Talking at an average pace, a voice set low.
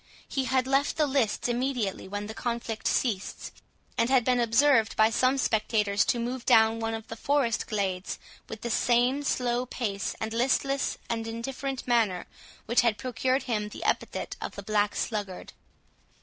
No: average, 165 wpm; high, 235 Hz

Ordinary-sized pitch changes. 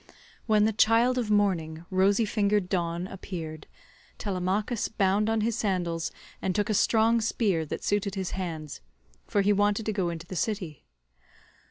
Yes: average, 3.2 semitones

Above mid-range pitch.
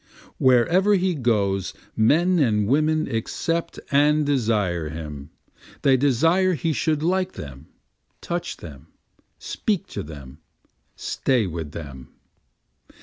No: low, 125 Hz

